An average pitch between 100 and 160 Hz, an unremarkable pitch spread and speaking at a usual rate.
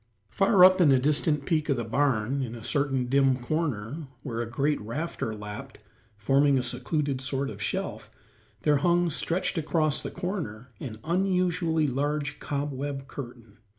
Yes: medium, 140 Hz; average, 4.0 semitones; average, 155 wpm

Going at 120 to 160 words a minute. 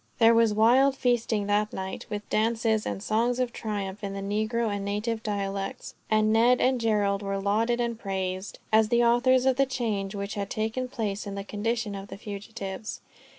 No: average, 190 wpm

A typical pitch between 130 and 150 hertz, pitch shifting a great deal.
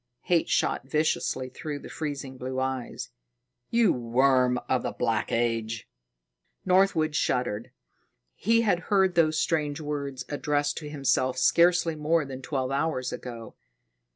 No: medium, 140 Hz; average, 3.9 semitones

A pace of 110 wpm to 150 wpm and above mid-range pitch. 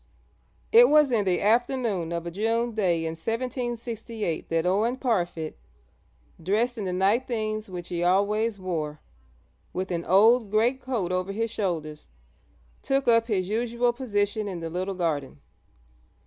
Yes: average, 145 wpm; high, 205 Hz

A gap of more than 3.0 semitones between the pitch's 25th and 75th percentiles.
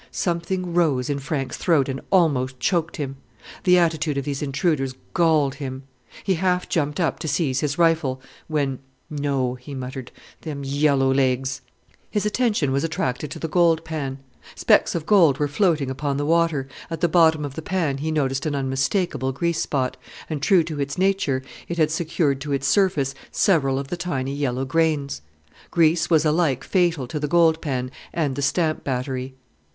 Yes: average, 3.6 semitones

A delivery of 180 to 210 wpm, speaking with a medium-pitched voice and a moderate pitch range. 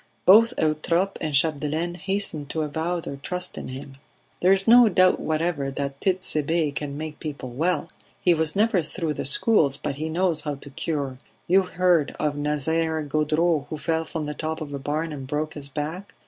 Yes: average, 190 wpm; medium, 155 Hz; average, 3.2 semitones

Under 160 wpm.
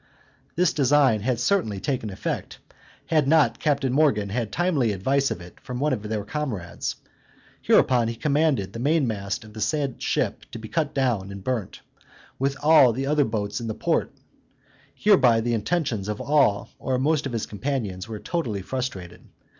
No: average, 170 wpm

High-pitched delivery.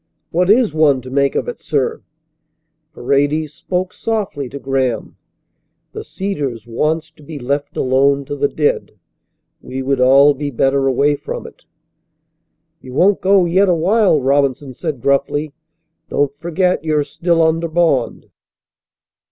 No: medium, 145 Hz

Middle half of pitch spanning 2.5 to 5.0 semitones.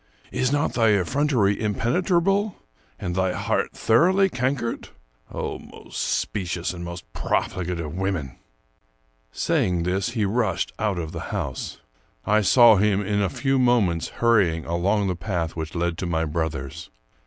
No: wide, 5.5 semitones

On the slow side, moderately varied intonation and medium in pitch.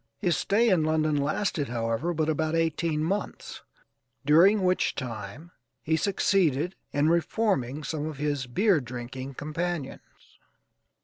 Yes: slow, 125 wpm; average, 3.9 semitones; medium, 155 Hz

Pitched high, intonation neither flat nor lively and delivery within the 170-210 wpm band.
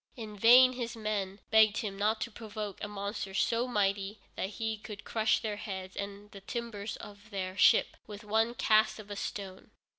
No: high, 210 Hz; narrow, 1.8 semitones; average, 185 wpm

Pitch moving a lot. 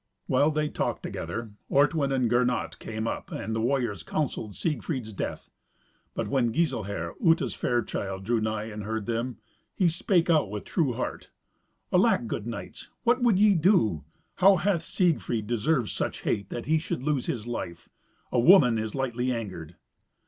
Yes: wide, 6.1 semitones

